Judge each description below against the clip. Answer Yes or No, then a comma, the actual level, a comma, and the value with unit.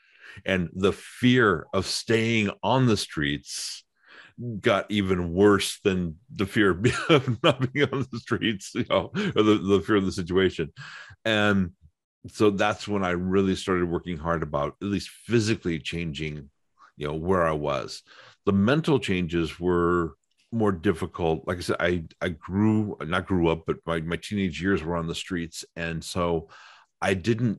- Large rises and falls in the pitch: No, average, 3.8 semitones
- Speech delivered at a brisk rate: No, average, 165 wpm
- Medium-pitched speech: No, very low, 95 Hz